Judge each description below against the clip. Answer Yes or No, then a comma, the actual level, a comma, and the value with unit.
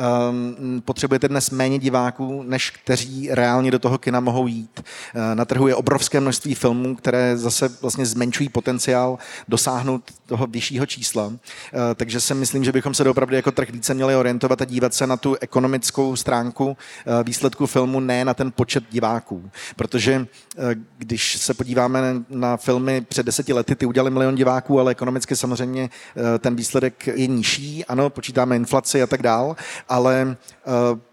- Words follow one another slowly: No, average, 155 wpm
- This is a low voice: Yes, low, 130 Hz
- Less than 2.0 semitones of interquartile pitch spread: Yes, narrow, 1.5 semitones